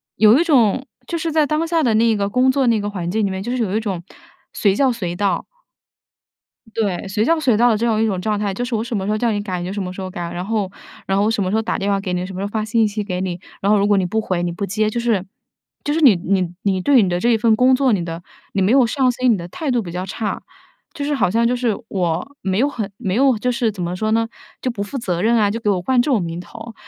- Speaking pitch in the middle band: No, high, 215 Hz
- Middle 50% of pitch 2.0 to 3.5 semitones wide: No, average, 4.0 semitones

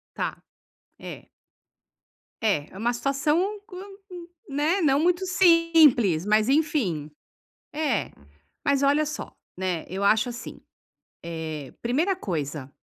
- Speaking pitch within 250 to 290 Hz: Yes, very high, 270 Hz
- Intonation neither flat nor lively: No, wide, 9.0 semitones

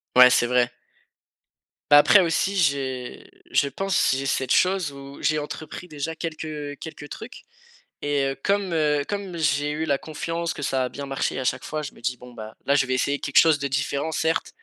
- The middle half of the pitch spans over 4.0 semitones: No, average, 3.0 semitones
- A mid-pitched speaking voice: Yes, medium, 145 Hz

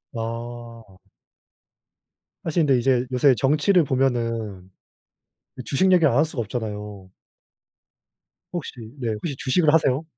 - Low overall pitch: Yes, low, 125 Hz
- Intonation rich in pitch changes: No, average, 4.5 semitones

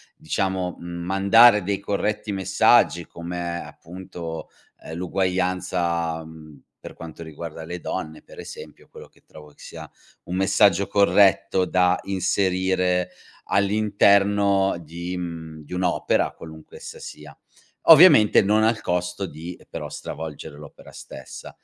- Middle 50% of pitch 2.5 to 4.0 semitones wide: Yes, average, 2.9 semitones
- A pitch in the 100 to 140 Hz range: No, very low, 90 Hz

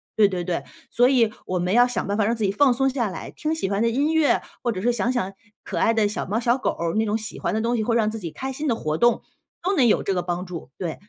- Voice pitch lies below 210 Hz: No, high, 225 Hz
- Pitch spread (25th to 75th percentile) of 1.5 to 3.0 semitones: No, average, 4.2 semitones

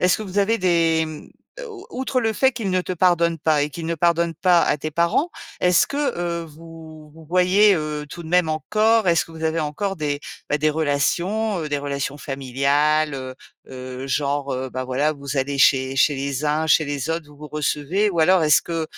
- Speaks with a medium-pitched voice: Yes, medium, 160 Hz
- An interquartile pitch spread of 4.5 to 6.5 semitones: No, average, 3.7 semitones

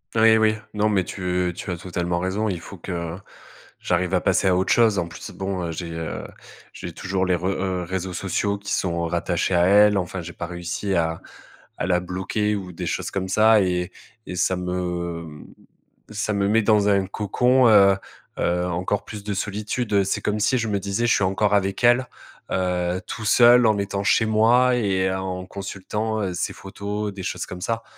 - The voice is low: Yes, very low, 95 Hz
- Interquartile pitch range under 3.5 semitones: Yes, average, 2.8 semitones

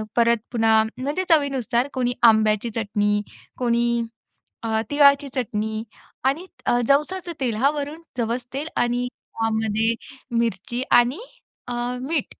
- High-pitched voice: Yes, high, 240 Hz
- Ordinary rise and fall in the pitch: Yes, average, 3.7 semitones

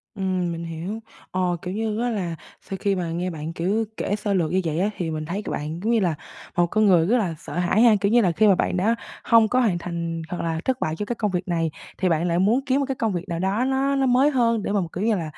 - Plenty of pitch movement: No, average, 4.7 semitones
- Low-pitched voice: No, high, 190 Hz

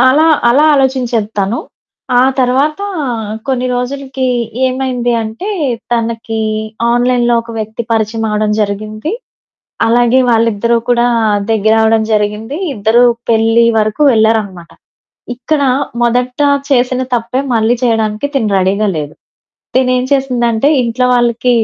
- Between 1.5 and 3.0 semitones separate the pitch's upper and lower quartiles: Yes, narrow, 2.5 semitones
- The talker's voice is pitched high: Yes, high, 235 Hz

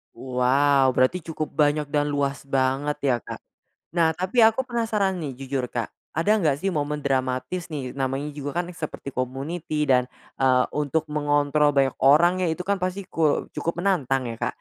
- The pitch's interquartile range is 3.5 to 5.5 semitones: Yes, average, 3.9 semitones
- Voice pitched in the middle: Yes, medium, 145 Hz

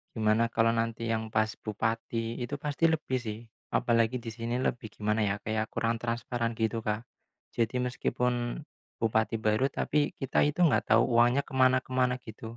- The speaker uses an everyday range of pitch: No, narrow, 2.0 semitones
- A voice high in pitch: No, low, 115 Hz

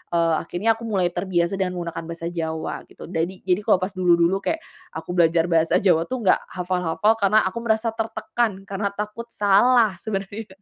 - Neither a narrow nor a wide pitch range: Yes, average, 3.9 semitones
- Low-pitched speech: No, high, 190 Hz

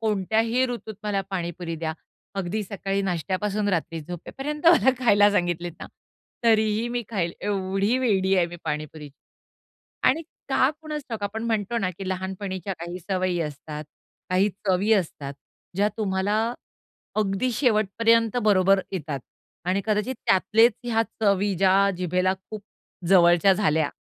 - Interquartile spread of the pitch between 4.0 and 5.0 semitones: No, average, 3.3 semitones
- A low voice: No, high, 195 Hz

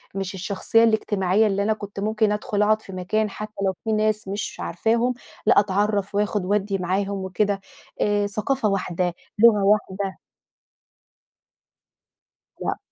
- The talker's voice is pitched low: No, high, 205 Hz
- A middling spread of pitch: No, narrow, 1.8 semitones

